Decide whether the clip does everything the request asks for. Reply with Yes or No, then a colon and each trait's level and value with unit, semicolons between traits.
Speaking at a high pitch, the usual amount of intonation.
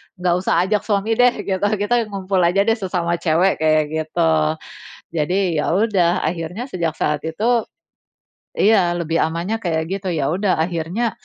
No: medium, 180 Hz; average, 3.7 semitones